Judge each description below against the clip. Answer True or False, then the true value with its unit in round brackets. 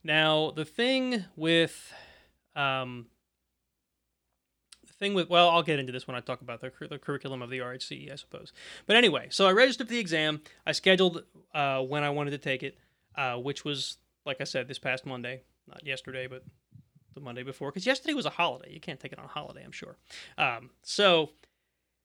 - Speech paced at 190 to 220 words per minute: True (200 wpm)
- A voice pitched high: False (140 Hz)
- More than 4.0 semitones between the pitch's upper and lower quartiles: True (4.6 semitones)